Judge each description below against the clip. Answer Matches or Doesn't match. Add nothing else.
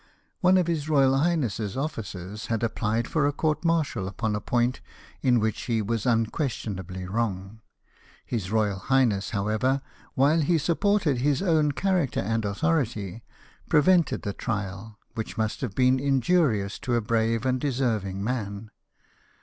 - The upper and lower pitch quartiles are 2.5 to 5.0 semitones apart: Doesn't match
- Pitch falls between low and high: Doesn't match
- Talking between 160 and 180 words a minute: Doesn't match